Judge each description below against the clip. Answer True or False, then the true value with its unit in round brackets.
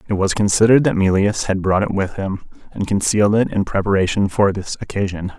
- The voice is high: False (100 Hz)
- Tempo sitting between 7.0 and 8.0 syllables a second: False (6.0 syllables/s)